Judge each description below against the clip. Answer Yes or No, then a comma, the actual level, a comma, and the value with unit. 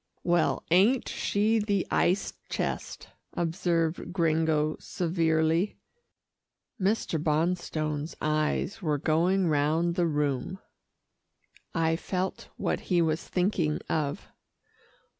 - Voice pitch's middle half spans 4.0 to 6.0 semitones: No, average, 2.9 semitones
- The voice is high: No, medium, 165 Hz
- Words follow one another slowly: Yes, slow, 95 wpm